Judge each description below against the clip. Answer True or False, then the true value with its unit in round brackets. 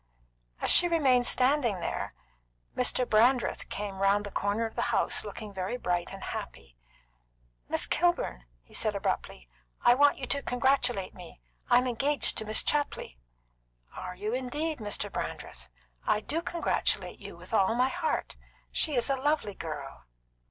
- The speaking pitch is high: True (240 Hz)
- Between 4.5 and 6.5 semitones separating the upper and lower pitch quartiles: True (5.6 semitones)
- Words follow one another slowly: False (155 wpm)